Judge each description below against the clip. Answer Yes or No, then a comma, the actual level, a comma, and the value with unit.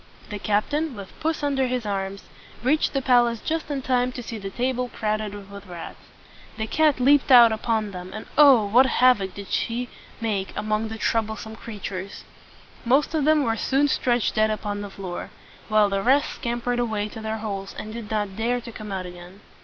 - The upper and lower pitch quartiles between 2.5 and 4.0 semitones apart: Yes, average, 3.6 semitones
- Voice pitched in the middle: No, high, 220 Hz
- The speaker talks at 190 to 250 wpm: Yes, average, 200 wpm